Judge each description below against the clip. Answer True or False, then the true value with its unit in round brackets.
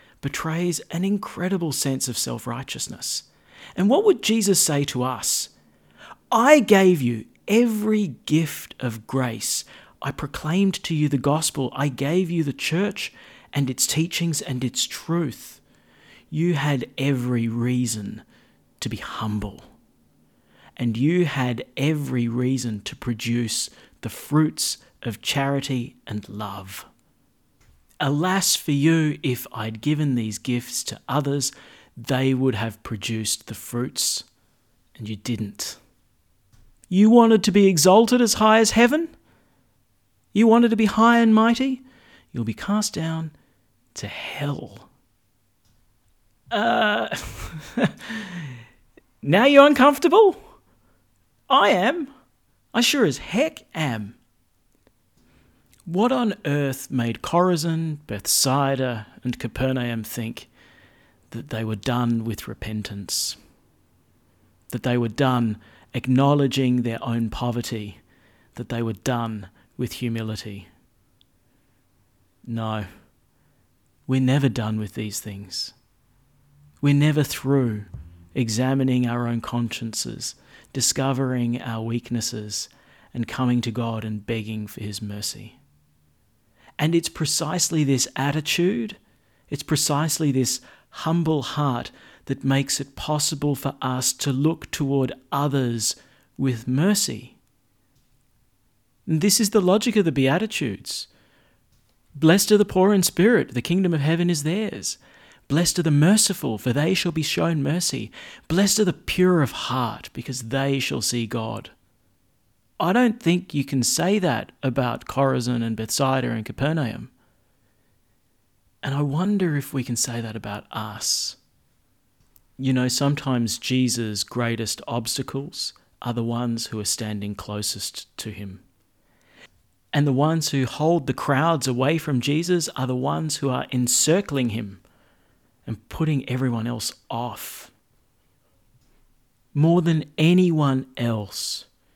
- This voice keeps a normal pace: False (125 wpm)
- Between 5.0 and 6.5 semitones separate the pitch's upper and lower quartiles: True (5.6 semitones)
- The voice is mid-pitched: False (130 Hz)